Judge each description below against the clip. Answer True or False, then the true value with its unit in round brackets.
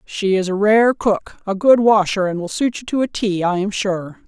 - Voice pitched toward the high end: True (205 Hz)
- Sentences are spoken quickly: True (255 wpm)